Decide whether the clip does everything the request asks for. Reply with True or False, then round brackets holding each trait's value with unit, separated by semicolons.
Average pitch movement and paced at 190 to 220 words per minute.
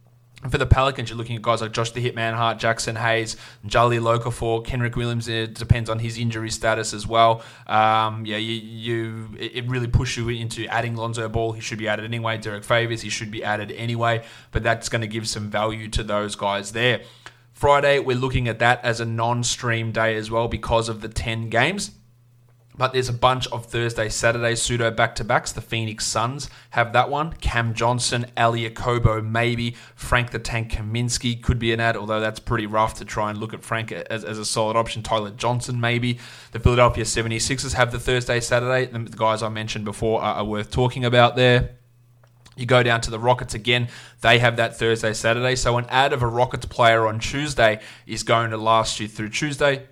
False (1.5 semitones; 200 wpm)